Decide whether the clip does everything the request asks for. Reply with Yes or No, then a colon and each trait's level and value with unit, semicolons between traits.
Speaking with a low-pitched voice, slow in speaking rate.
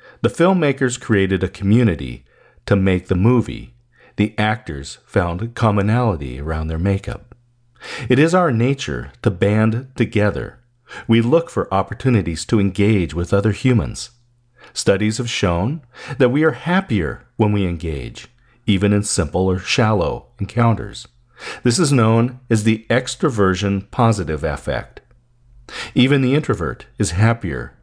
Yes: low, 110 Hz; slow, 130 wpm